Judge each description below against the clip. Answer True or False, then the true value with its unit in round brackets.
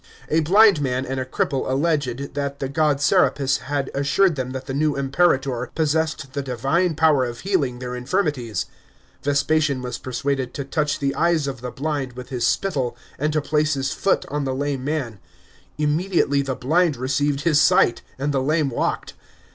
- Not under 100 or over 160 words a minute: False (180 wpm)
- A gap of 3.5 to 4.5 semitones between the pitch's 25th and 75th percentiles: False (2.8 semitones)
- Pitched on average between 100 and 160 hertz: True (140 Hz)